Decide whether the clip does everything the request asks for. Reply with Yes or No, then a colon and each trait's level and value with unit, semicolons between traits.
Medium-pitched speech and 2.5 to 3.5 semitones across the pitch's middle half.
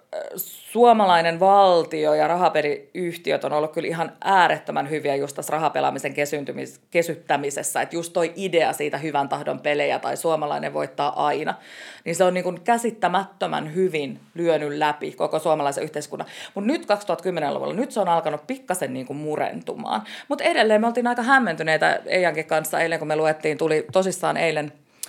No: medium, 165 Hz; average, 4.0 semitones